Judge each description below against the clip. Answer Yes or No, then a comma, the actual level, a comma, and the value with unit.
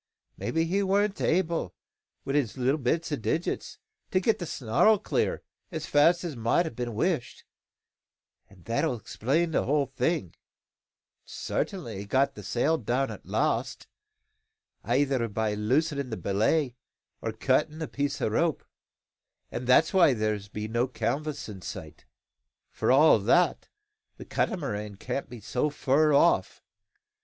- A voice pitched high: No, low, 135 Hz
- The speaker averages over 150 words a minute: No, average, 145 wpm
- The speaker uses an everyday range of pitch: No, wide, 6.0 semitones